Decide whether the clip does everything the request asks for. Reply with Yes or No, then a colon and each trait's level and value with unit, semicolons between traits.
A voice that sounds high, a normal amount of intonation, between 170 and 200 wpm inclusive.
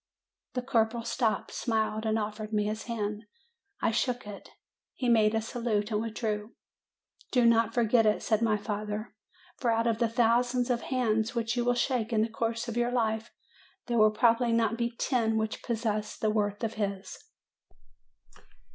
No: high, 225 Hz; narrow, 1.7 semitones; average, 175 wpm